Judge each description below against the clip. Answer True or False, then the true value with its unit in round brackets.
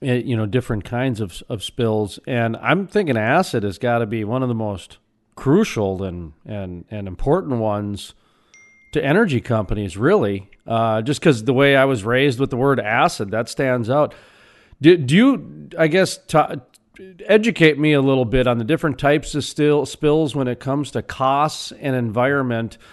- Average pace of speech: True (180 wpm)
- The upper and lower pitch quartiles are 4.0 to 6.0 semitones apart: True (5.0 semitones)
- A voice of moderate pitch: False (125 Hz)